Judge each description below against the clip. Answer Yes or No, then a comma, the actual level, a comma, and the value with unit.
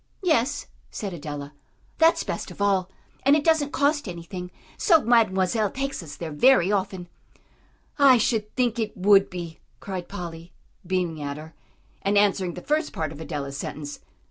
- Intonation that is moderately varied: No, wide, 6.5 semitones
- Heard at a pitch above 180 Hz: Yes, high, 190 Hz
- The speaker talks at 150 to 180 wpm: Yes, average, 160 wpm